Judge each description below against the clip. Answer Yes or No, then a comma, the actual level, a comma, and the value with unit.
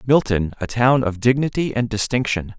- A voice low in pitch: Yes, low, 120 Hz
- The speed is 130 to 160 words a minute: Yes, average, 140 wpm